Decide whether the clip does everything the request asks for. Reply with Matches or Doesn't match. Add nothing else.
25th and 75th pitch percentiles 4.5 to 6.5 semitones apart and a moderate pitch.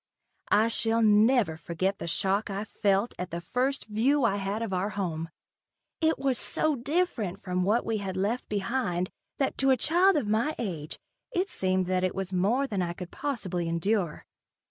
Doesn't match